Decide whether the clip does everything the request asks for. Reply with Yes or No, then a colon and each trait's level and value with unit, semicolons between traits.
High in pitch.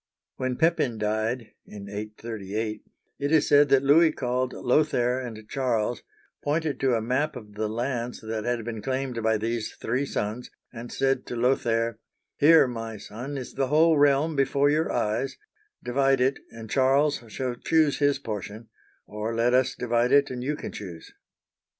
No: low, 125 Hz